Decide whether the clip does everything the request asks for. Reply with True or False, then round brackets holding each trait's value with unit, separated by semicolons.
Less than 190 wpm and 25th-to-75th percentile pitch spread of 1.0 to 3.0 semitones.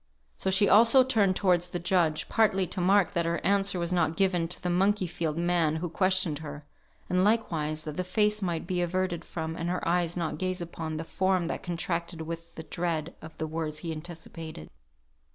False (195 wpm; 2.5 semitones)